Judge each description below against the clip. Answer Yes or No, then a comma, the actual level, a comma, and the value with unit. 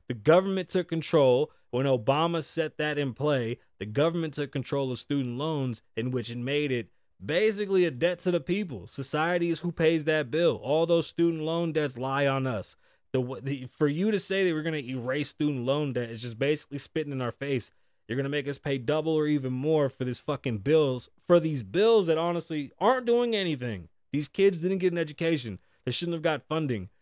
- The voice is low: No, medium, 150 Hz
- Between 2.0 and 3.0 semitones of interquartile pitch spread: No, average, 4.3 semitones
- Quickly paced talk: Yes, fast, 215 wpm